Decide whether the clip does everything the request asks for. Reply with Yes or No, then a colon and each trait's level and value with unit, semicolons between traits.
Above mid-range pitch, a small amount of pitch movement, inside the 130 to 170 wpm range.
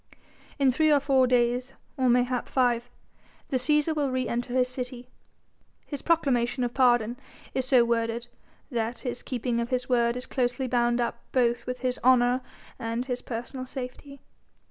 Yes: very high, 250 Hz; narrow, 1.3 semitones; average, 165 wpm